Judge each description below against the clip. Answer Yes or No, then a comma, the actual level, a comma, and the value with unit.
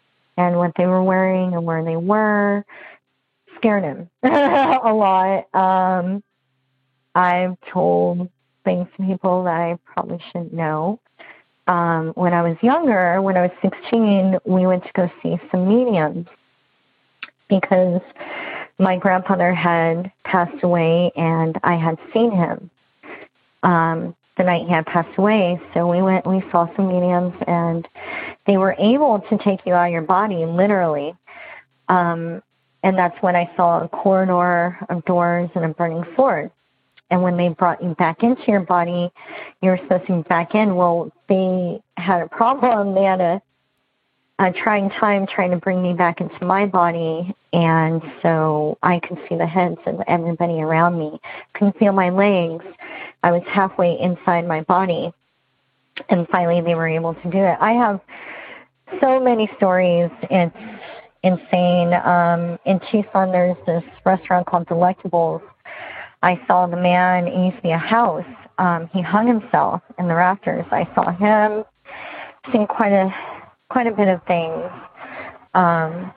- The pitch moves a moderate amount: No, narrow, 2.1 semitones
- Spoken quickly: No, average, 160 wpm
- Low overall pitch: No, medium, 180 Hz